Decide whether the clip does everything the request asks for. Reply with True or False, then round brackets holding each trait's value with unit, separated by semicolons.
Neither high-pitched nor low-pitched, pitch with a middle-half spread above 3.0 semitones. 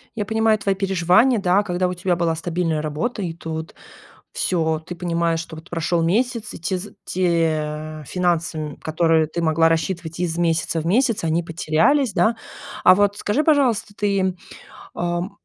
True (175 Hz; 3.6 semitones)